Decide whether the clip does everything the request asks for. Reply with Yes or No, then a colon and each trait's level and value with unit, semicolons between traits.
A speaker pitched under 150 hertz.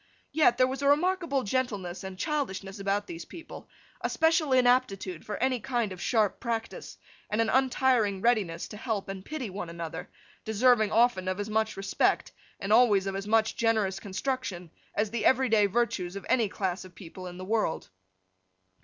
No: high, 215 Hz